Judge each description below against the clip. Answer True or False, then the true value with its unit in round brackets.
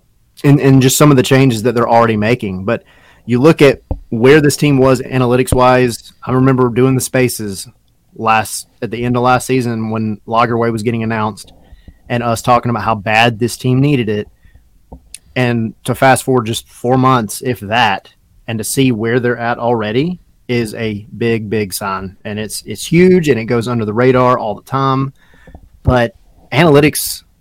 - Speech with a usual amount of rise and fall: True (3.0 semitones)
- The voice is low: True (120 Hz)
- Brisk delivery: False (180 wpm)